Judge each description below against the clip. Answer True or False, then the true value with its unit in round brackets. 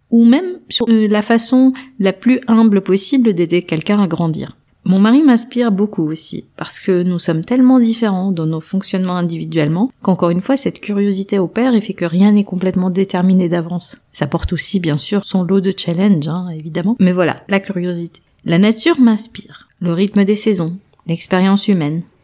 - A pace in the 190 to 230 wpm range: False (180 wpm)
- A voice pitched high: True (195 Hz)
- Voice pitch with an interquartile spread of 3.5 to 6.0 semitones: True (3.9 semitones)